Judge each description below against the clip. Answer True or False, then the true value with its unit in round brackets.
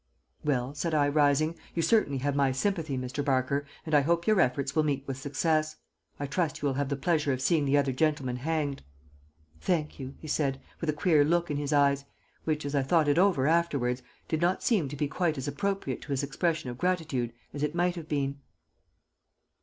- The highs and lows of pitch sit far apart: False (2.9 semitones)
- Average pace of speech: False (210 wpm)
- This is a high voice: False (145 Hz)